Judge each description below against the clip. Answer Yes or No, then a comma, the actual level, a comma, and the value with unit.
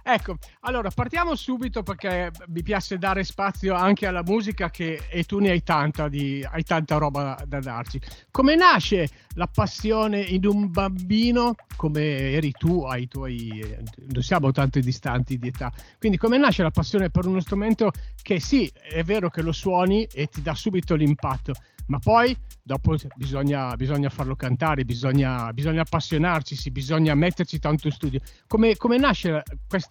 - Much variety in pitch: Yes, wide, 6.2 semitones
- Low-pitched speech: No, medium, 160 Hz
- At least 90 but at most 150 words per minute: No, average, 165 wpm